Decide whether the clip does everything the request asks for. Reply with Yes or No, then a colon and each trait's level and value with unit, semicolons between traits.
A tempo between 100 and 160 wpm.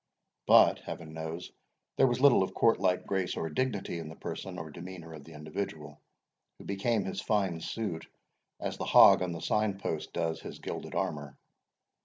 No: average, 175 wpm